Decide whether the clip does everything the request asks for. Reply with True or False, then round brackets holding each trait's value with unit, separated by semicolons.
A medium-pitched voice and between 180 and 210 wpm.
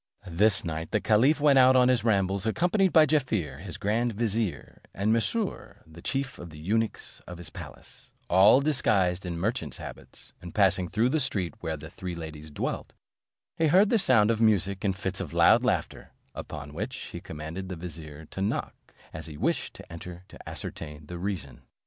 False (95 Hz; 185 wpm)